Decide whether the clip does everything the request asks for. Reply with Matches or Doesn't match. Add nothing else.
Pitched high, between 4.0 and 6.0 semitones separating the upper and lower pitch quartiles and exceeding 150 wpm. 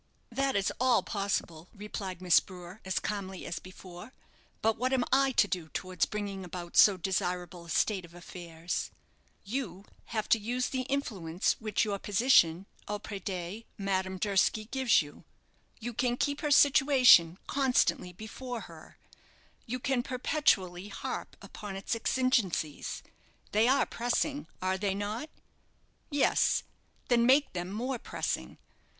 Doesn't match